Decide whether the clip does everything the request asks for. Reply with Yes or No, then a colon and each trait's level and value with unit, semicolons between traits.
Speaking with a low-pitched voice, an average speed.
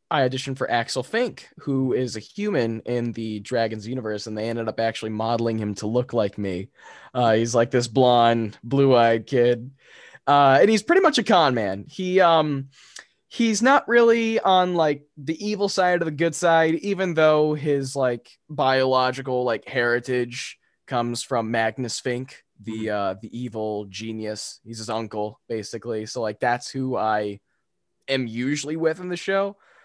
Yes: low, 125 Hz; average, 170 wpm